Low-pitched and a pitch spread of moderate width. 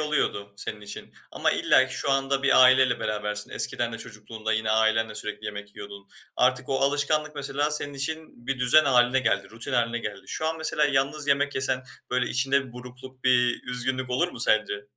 Yes: low, 125 Hz; average, 3.8 semitones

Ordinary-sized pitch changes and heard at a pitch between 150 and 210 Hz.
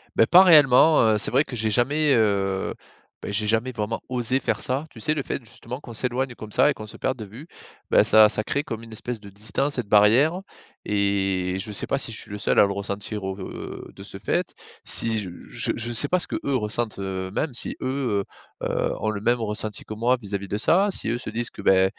No: average, 4.0 semitones; low, 110 Hz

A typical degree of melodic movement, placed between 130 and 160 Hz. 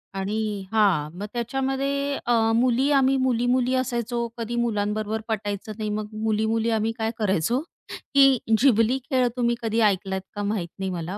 No: average, 3.2 semitones; high, 225 Hz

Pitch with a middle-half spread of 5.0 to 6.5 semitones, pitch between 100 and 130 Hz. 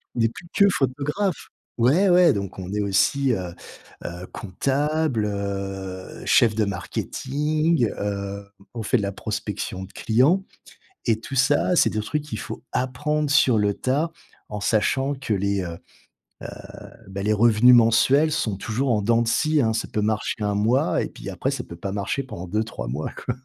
Yes: wide, 5.6 semitones; low, 115 Hz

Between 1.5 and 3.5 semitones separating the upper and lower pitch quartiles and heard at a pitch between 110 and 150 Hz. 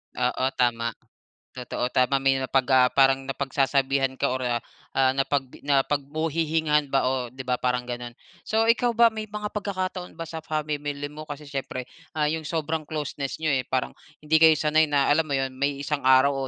Yes: average, 3.1 semitones; medium, 140 Hz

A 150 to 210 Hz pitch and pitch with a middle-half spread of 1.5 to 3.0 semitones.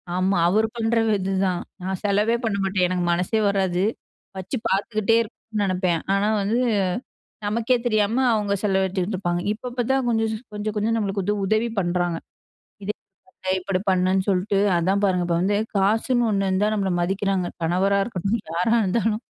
Yes: high, 195 Hz; narrow, 2.6 semitones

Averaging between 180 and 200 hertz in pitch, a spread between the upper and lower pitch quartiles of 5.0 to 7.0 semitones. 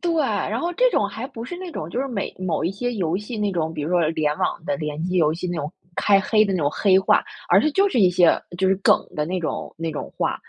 Yes: high, 190 Hz; wide, 5.5 semitones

